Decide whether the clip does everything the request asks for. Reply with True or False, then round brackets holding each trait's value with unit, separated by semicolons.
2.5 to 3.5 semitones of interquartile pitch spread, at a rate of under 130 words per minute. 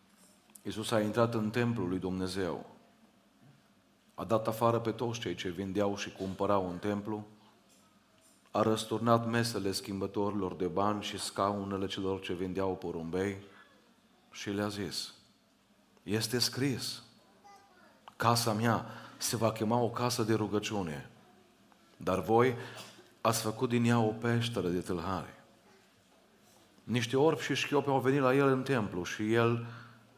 False (3.2 semitones; 135 wpm)